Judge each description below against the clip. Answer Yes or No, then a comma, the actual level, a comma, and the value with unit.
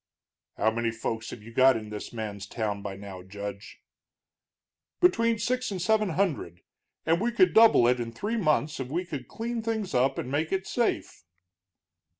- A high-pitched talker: No, low, 135 Hz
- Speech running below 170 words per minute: No, average, 175 wpm